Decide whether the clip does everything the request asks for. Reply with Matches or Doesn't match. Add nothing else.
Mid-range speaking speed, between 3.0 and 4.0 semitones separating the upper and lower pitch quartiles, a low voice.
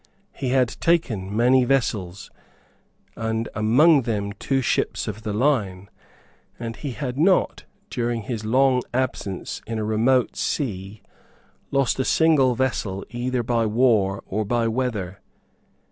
Doesn't match